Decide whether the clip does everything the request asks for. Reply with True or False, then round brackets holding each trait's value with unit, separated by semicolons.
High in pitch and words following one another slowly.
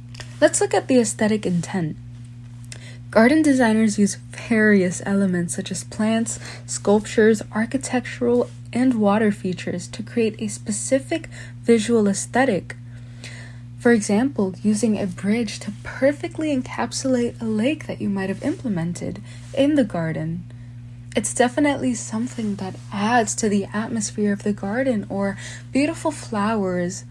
True (195 Hz; 125 wpm)